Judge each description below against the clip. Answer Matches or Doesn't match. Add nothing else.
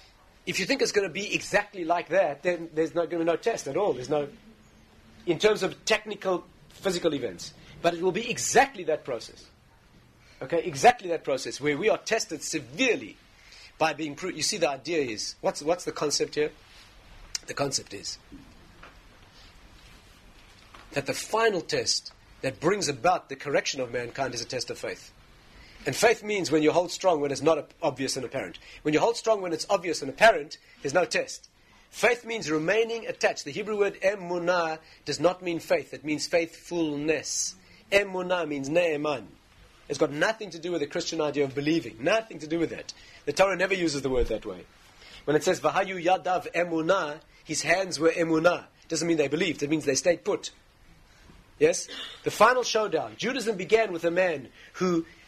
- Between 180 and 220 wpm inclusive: Matches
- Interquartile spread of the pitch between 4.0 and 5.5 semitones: Matches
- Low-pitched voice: Doesn't match